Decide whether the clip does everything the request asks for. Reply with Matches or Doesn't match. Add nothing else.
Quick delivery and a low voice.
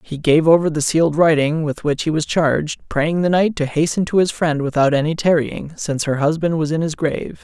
Doesn't match